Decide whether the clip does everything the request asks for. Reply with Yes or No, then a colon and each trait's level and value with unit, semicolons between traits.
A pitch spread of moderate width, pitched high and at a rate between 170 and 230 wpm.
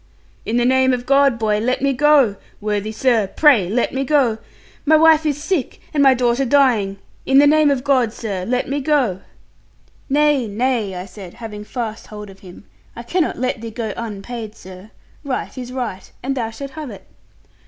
Yes: average, 4.4 semitones; high, 245 Hz; average, 190 wpm